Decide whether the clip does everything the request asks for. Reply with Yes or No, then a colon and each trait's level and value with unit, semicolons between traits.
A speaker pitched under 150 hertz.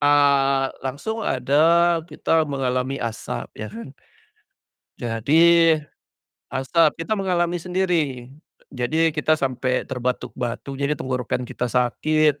Yes: medium, 140 Hz